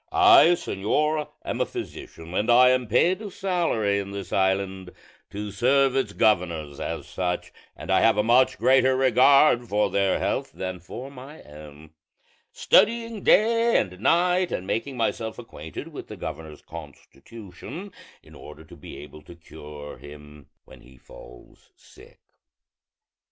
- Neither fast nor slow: Yes, average, 150 wpm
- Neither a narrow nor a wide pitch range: No, wide, 8.2 semitones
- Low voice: Yes, low, 105 Hz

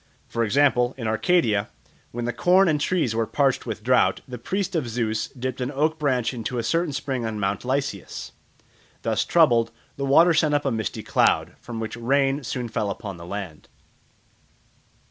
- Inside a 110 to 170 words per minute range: No, average, 180 wpm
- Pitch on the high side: No, low, 125 Hz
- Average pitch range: Yes, average, 4.2 semitones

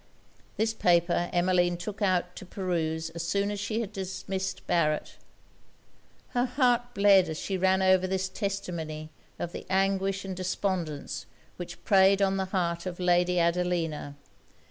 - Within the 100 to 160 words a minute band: Yes, average, 145 wpm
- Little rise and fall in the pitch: Yes, narrow, 2.1 semitones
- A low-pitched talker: No, medium, 185 Hz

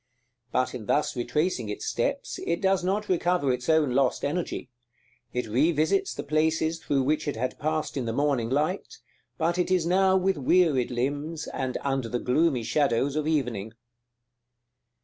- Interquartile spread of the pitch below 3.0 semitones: No, average, 4.8 semitones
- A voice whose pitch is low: No, medium, 150 Hz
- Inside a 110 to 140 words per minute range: No, average, 165 wpm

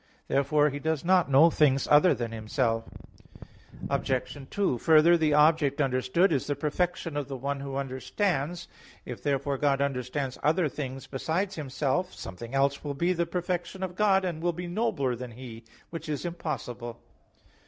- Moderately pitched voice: Yes, medium, 145 Hz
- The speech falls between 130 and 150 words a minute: No, average, 165 wpm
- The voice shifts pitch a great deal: No, average, 4.3 semitones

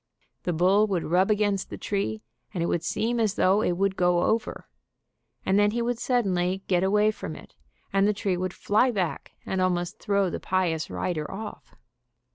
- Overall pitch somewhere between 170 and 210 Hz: Yes, high, 190 Hz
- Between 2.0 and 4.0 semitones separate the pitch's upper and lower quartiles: Yes, average, 2.8 semitones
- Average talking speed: Yes, average, 190 wpm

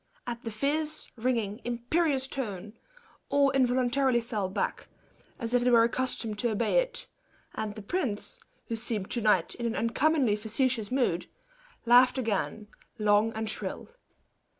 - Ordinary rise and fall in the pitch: Yes, average, 3.2 semitones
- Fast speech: No, average, 145 wpm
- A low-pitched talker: No, high, 235 Hz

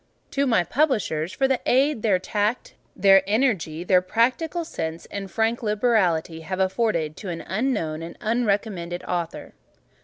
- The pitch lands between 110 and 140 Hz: No, high, 200 Hz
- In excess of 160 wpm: No, slow, 135 wpm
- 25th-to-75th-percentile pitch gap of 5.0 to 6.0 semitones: Yes, wide, 5.4 semitones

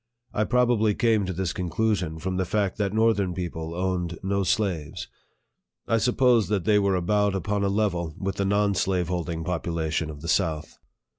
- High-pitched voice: No, very low, 95 Hz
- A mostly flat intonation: No, average, 3.3 semitones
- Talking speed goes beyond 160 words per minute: Yes, average, 175 wpm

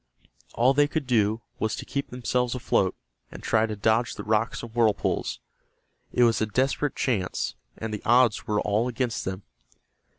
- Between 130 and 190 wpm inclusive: Yes, average, 170 wpm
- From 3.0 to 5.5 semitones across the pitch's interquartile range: No, narrow, 2.6 semitones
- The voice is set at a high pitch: No, low, 115 Hz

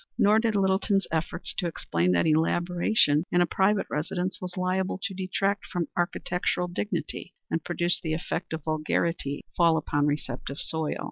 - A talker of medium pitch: Yes, medium, 175 Hz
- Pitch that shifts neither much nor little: Yes, average, 3.1 semitones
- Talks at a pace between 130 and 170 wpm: Yes, average, 160 wpm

